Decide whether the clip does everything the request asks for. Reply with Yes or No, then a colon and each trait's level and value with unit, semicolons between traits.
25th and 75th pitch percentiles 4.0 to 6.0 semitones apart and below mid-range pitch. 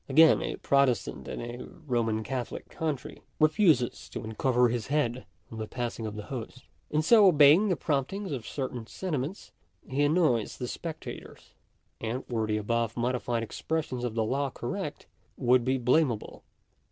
Yes: average, 4.3 semitones; low, 130 Hz